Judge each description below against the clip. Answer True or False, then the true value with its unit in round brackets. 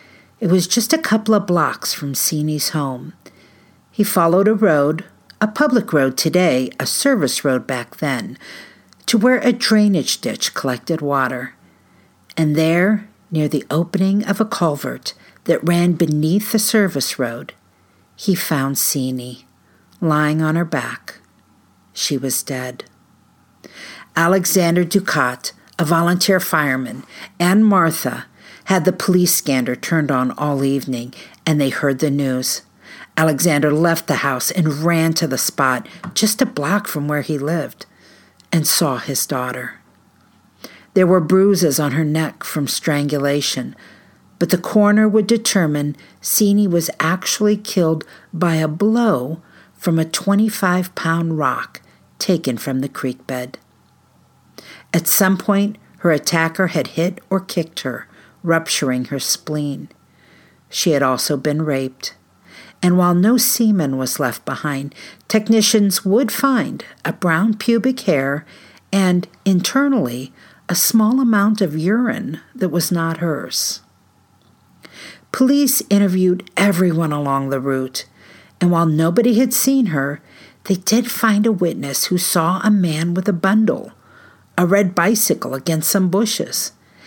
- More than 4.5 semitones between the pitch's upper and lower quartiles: True (5.6 semitones)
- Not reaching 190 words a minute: True (135 wpm)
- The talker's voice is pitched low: False (170 Hz)